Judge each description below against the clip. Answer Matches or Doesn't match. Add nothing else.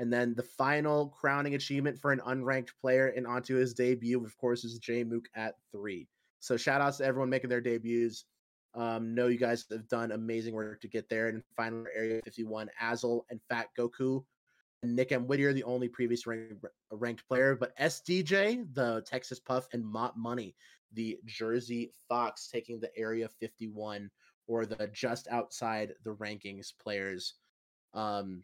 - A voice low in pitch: Matches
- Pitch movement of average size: Doesn't match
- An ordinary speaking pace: Matches